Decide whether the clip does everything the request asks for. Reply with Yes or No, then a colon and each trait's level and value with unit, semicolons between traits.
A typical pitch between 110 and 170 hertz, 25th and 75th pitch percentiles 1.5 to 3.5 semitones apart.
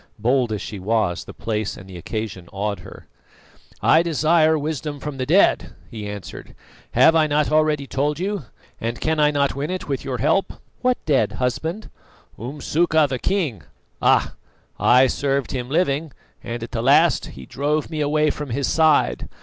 No: medium, 140 Hz; average, 4.9 semitones